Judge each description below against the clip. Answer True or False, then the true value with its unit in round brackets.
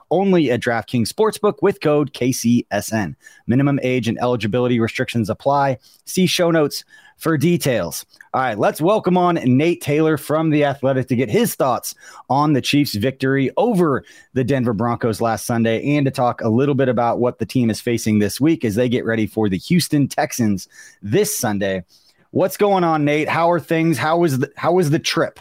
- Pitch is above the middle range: False (135 Hz)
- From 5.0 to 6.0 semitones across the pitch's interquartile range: True (5.3 semitones)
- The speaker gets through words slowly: False (190 wpm)